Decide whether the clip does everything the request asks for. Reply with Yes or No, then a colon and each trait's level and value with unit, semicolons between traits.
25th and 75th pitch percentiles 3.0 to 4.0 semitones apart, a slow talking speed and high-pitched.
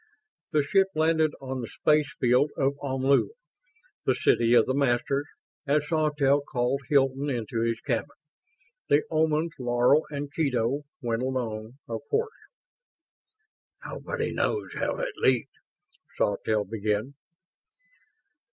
No: average, 3.6 semitones; slow, 120 wpm; low, 135 Hz